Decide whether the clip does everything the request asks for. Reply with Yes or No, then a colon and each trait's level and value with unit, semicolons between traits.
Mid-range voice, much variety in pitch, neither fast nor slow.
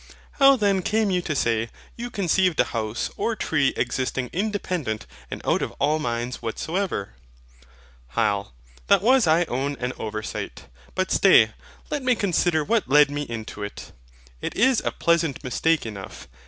Yes: medium, 155 Hz; wide, 8.8 semitones; average, 155 wpm